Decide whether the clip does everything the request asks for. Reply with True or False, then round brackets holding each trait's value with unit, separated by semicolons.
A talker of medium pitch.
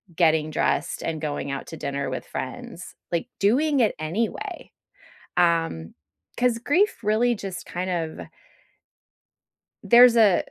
True (180 Hz)